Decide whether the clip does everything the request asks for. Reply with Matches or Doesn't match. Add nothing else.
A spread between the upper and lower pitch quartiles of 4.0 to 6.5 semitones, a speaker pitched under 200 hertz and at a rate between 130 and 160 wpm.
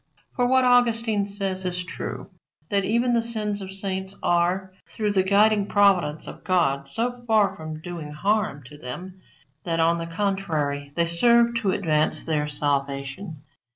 Matches